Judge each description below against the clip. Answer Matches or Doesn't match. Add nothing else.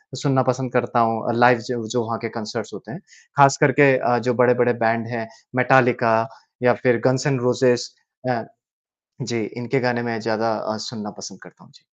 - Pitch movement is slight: Matches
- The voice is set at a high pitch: Doesn't match